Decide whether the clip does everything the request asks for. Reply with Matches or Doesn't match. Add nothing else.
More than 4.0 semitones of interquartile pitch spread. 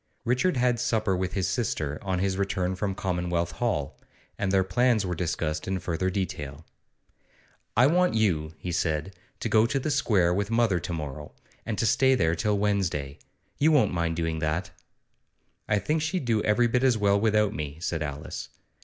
Matches